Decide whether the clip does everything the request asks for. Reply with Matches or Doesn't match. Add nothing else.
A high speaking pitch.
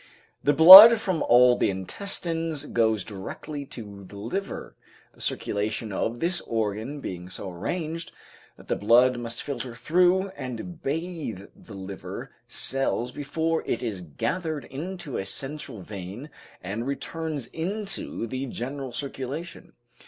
Doesn't match